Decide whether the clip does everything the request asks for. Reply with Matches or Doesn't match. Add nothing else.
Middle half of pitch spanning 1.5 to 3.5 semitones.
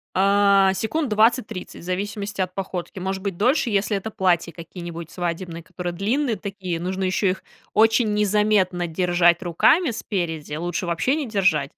Matches